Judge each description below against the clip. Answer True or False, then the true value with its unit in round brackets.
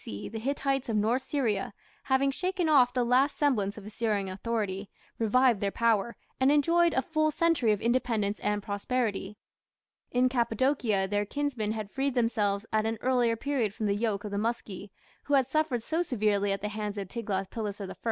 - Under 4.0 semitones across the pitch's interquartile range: False (4.4 semitones)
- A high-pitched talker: True (230 Hz)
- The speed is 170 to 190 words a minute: True (185 wpm)